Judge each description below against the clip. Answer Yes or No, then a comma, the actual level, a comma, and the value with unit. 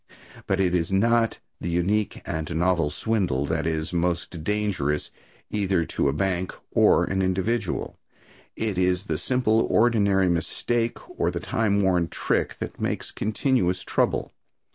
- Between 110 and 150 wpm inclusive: Yes, average, 140 wpm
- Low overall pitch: Yes, very low, 95 Hz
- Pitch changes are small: No, average, 3.7 semitones